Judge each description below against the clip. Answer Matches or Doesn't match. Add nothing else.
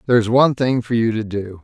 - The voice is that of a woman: Doesn't match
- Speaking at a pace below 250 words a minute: Doesn't match